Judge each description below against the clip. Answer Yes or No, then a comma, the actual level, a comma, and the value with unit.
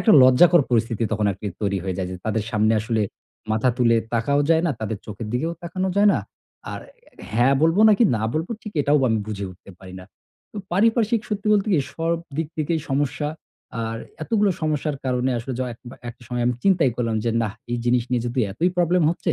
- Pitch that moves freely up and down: Yes, wide, 7.0 semitones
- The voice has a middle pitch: No, low, 130 Hz